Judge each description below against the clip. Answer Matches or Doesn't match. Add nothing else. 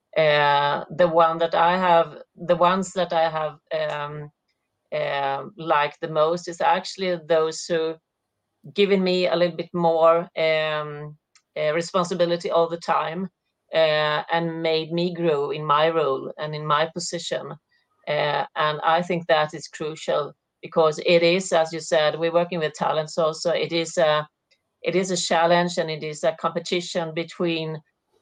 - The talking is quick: Doesn't match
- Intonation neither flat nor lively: Doesn't match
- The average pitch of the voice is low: Doesn't match